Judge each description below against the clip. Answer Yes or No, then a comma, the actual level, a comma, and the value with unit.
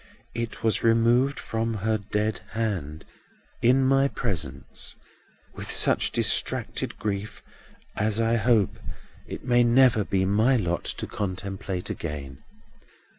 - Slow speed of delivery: Yes, slow, 120 wpm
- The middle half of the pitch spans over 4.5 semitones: No, average, 3.3 semitones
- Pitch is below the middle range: Yes, low, 110 Hz